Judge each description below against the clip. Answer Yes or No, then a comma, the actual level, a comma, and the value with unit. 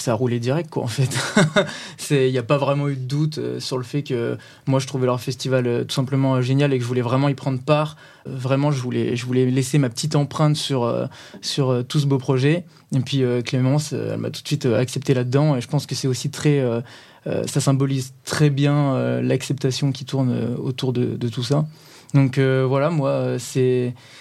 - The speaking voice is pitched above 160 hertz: No, low, 135 Hz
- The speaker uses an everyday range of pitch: No, narrow, 2.1 semitones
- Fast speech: Yes, fast, 240 wpm